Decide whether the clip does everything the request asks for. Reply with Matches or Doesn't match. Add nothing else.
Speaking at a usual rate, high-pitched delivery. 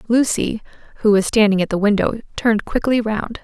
Matches